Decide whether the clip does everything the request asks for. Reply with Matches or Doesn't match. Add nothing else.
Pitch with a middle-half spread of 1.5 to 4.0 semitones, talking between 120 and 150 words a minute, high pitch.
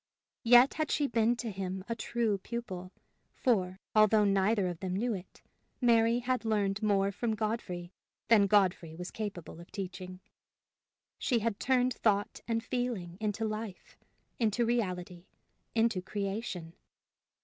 Matches